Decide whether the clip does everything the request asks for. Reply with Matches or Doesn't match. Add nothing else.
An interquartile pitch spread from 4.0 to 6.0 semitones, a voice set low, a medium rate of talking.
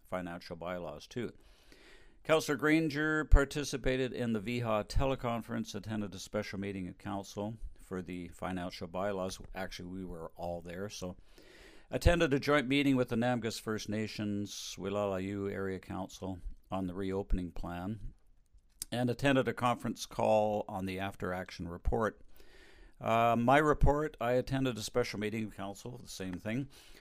Matches